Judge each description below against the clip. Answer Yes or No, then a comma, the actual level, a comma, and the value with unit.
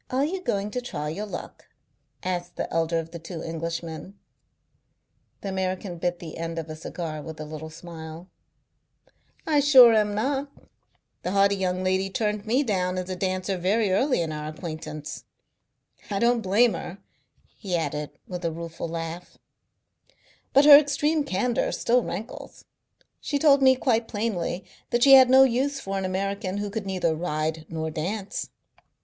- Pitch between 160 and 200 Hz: Yes, medium, 185 Hz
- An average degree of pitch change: No, wide, 5.8 semitones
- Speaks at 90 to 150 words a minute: No, average, 165 wpm